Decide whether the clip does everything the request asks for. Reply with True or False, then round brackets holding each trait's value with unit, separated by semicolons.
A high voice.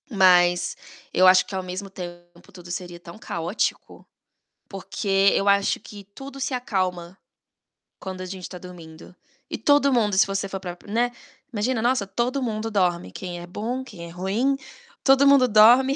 True (195 Hz)